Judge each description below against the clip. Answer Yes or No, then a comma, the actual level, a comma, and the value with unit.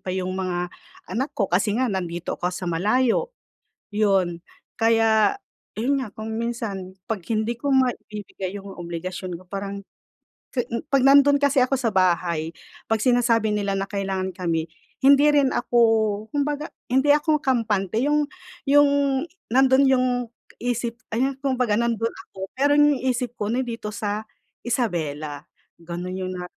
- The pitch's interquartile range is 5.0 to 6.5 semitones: Yes, wide, 5.4 semitones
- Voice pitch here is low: No, high, 220 Hz